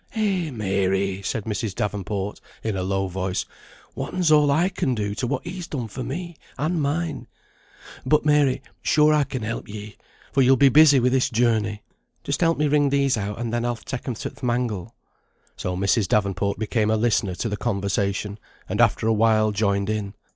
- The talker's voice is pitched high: No, low, 115 Hz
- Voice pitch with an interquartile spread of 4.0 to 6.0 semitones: Yes, wide, 5.5 semitones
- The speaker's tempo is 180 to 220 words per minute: Yes, average, 190 wpm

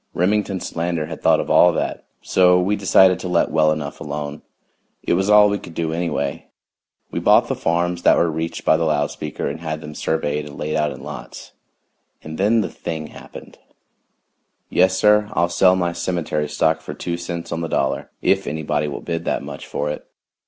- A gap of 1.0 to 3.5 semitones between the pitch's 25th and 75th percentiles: Yes, average, 2.7 semitones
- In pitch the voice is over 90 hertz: No, very low, 85 Hz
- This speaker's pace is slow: No, average, 200 wpm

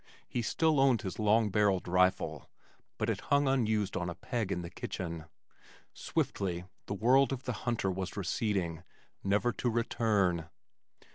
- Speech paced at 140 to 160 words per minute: Yes, average, 150 wpm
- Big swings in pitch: No, average, 4.6 semitones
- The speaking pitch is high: No, low, 105 Hz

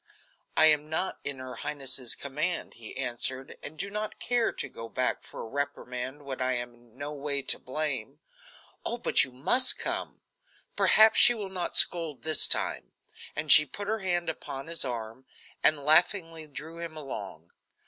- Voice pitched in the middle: Yes, medium, 145 Hz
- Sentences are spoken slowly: No, average, 175 wpm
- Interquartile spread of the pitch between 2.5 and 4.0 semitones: No, average, 4.5 semitones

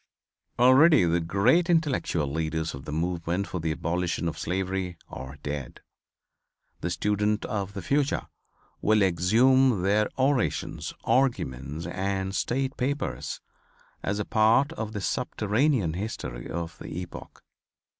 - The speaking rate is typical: No, slow, 125 wpm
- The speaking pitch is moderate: No, very low, 95 Hz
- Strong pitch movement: Yes, wide, 6.5 semitones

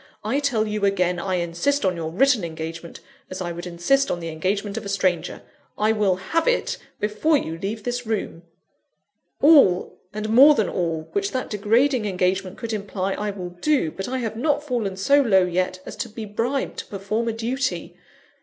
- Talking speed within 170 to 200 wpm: Yes, average, 190 wpm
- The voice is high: Yes, high, 210 Hz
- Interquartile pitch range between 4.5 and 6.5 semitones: Yes, average, 5.2 semitones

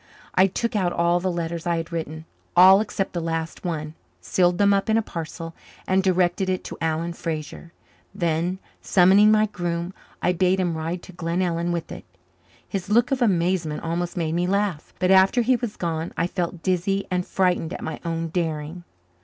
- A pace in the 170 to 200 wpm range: Yes, average, 185 wpm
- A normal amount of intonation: No, narrow, 2.3 semitones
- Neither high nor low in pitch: Yes, medium, 175 Hz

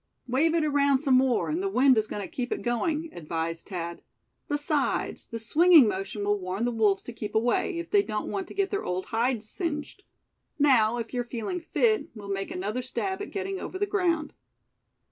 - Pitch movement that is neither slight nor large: No, wide, 7.6 semitones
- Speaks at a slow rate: No, average, 200 wpm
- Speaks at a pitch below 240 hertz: No, very high, 255 Hz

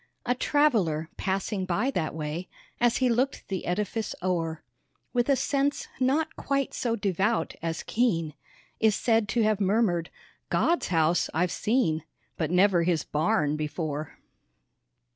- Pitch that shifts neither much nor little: No, wide, 6.4 semitones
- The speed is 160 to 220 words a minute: No, average, 140 wpm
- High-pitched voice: Yes, high, 195 Hz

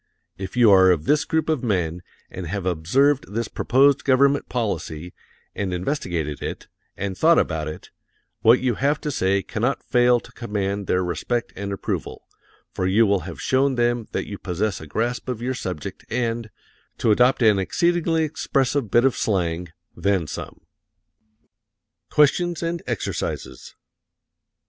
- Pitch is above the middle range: No, low, 115 Hz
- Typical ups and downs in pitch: No, wide, 6.1 semitones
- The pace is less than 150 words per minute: No, average, 155 wpm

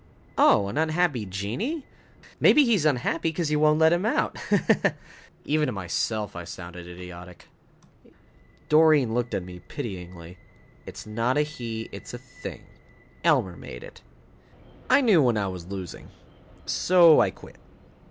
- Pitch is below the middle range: Yes, low, 115 Hz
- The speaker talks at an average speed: Yes, average, 150 wpm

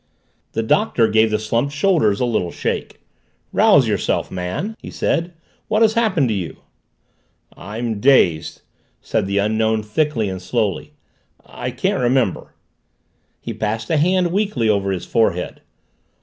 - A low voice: Yes, low, 110 Hz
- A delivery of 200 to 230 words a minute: No, average, 140 wpm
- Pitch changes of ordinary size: No, wide, 6.7 semitones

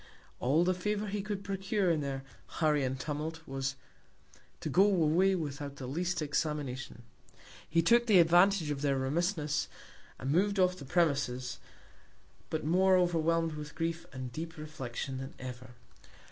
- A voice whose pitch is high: No, medium, 160 Hz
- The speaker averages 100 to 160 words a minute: Yes, average, 150 wpm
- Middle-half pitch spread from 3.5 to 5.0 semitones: Yes, average, 4.7 semitones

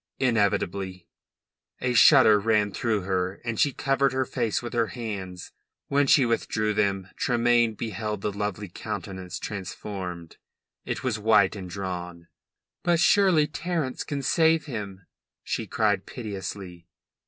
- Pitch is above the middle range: No, low, 105 Hz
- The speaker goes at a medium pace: No, slow, 130 wpm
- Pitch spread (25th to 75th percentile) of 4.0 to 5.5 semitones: Yes, average, 4.7 semitones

